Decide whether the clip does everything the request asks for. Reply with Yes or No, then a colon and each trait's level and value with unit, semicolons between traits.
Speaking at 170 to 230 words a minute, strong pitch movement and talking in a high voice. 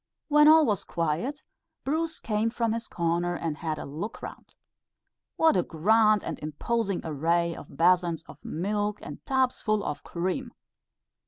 No: average, 155 wpm; wide, 5.7 semitones; high, 200 Hz